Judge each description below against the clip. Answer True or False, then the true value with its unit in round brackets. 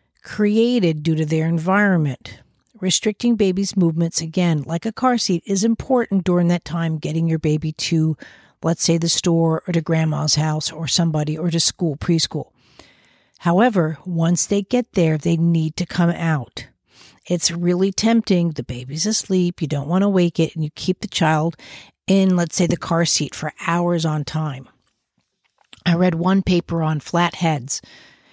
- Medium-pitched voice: True (170 Hz)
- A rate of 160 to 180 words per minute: True (170 wpm)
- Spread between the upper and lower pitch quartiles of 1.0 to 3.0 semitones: True (2.7 semitones)